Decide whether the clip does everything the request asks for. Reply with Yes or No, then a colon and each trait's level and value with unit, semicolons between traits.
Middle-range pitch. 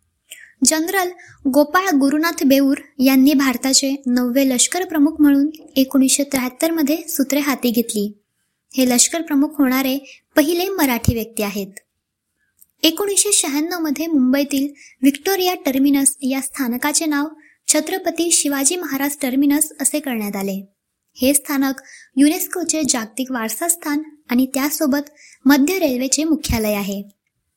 No: very high, 280 Hz